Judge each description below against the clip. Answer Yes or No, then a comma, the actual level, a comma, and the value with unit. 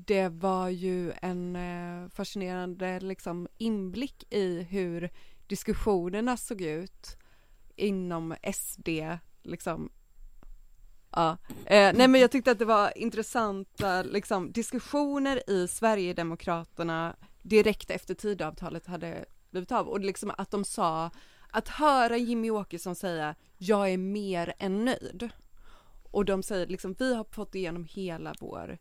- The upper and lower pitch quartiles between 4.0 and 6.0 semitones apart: No, average, 3.3 semitones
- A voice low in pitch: No, high, 195 Hz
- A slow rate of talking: Yes, slow, 130 wpm